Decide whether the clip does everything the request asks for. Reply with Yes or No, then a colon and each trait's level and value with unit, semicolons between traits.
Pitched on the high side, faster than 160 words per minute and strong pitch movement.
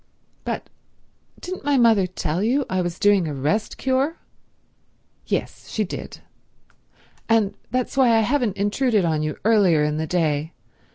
No: high, 205 Hz; average, 145 wpm; wide, 6.5 semitones